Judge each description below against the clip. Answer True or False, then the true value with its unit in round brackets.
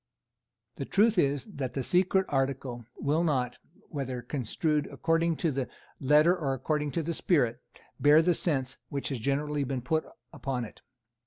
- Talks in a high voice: False (145 Hz)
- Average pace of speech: True (160 wpm)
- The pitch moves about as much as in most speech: True (3.6 semitones)